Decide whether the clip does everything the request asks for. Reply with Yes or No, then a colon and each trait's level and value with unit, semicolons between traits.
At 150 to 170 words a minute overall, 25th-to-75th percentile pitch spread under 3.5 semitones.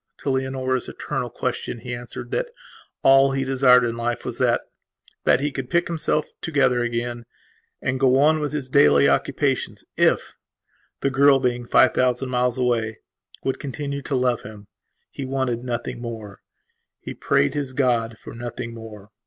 Yes: average, 155 wpm; narrow, 2.4 semitones